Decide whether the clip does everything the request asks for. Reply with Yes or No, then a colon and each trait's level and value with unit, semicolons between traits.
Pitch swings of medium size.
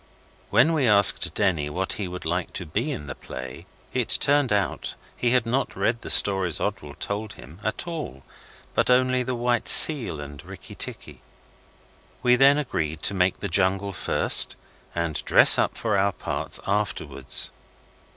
No: wide, 6.1 semitones